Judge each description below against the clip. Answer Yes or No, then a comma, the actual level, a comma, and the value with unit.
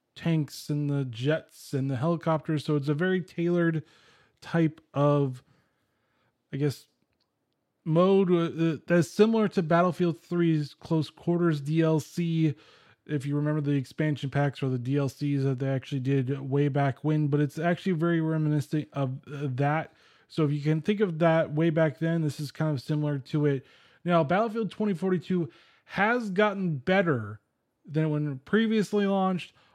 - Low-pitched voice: No, medium, 155 Hz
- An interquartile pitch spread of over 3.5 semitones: No, average, 3.2 semitones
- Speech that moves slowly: No, average, 150 wpm